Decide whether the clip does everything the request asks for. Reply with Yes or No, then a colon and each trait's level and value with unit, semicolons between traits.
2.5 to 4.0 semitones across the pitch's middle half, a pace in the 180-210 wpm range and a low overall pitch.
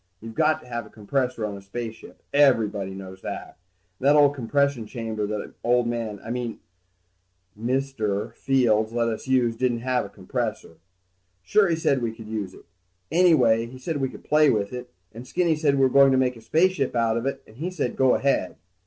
Yes: average, 3.7 semitones; fast, 205 wpm; low, 120 Hz